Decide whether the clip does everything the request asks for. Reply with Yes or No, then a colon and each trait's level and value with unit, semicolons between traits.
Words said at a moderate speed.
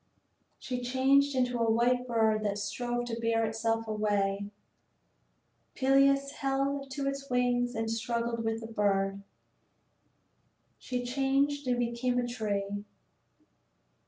No: slow, 120 wpm